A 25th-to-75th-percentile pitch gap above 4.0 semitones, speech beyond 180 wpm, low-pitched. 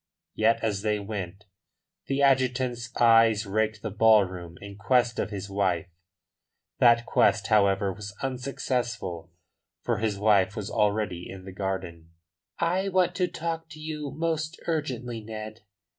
No: average, 4.6 semitones; average, 140 wpm; low, 110 Hz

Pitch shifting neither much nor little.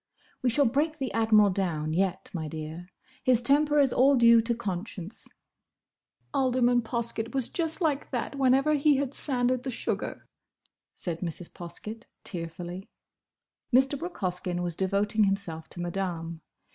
No: wide, 6.9 semitones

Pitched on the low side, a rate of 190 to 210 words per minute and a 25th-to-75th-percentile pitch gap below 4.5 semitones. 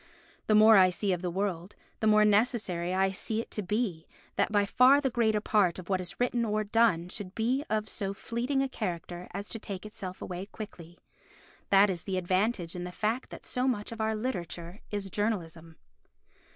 No: high, 205 Hz; average, 200 wpm; average, 3.5 semitones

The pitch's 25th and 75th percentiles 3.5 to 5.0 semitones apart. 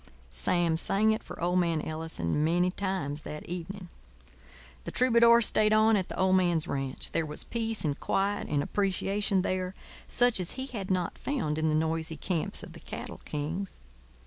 Yes: average, 4.3 semitones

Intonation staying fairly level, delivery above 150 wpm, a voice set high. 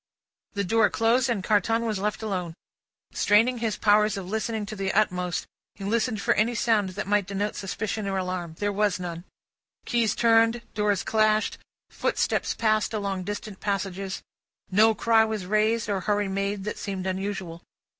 Yes: narrow, 2.3 semitones; average, 165 wpm; high, 205 Hz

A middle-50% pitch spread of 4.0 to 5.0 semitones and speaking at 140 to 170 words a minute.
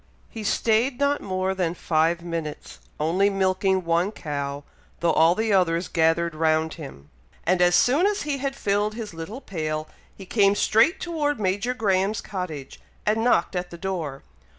Yes: average, 4.7 semitones; average, 165 wpm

